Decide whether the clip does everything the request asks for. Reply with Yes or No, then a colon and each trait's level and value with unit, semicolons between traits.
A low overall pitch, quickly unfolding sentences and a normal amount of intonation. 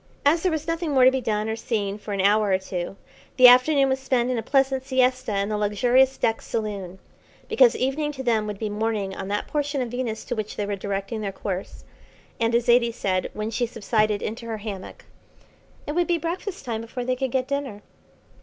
No: high, 230 Hz; fast, 220 wpm; average, 4.1 semitones